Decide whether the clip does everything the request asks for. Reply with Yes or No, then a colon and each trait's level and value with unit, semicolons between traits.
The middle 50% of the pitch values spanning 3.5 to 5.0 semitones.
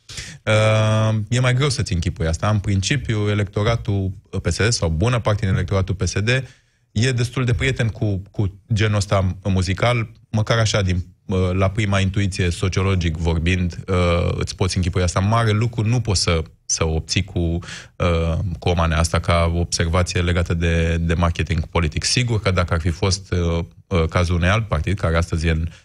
Yes: average, 4.0 semitones